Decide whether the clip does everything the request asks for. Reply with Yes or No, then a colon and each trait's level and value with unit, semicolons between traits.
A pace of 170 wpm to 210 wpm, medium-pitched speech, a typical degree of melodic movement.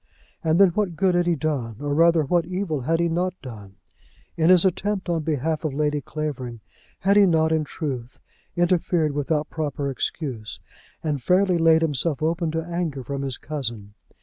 Yes: average, 175 wpm; medium, 160 Hz; average, 3.6 semitones